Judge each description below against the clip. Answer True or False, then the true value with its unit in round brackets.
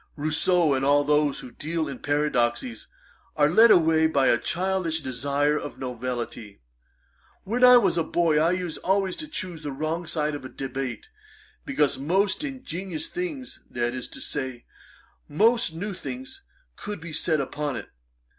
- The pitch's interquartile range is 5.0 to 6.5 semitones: True (5.3 semitones)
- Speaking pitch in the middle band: True (155 Hz)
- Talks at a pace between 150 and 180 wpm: True (160 wpm)